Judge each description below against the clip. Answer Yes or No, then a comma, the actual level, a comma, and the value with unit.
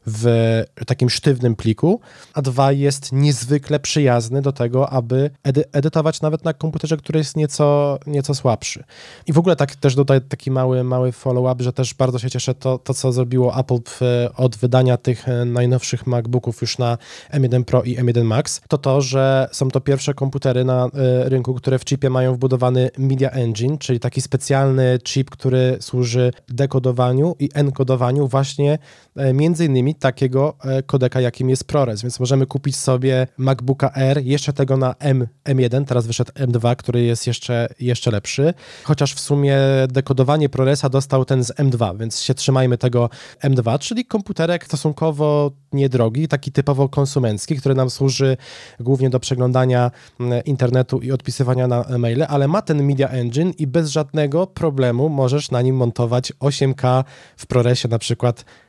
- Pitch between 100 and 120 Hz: No, low, 130 Hz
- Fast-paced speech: Yes, fast, 165 wpm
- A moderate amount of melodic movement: No, narrow, 2.1 semitones